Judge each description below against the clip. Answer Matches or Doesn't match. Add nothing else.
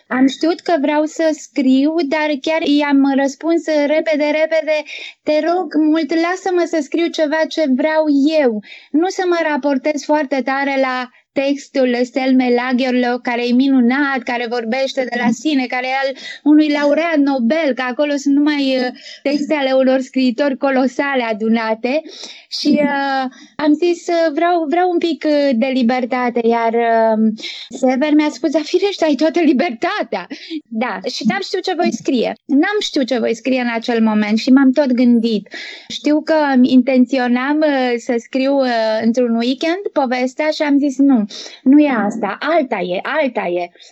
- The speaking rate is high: Doesn't match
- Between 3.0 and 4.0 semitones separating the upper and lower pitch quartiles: Matches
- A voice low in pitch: Doesn't match